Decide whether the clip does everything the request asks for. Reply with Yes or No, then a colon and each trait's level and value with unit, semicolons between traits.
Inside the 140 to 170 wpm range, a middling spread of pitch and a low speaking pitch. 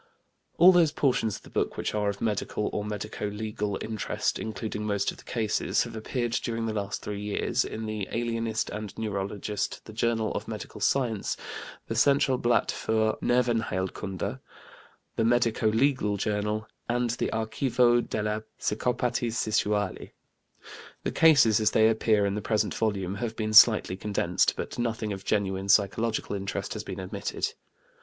No: average, 155 wpm; narrow, 2.0 semitones; low, 110 Hz